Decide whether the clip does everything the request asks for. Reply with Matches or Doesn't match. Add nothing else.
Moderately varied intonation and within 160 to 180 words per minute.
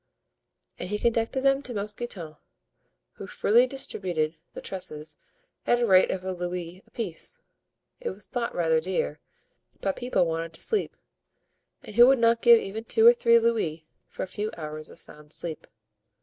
Doesn't match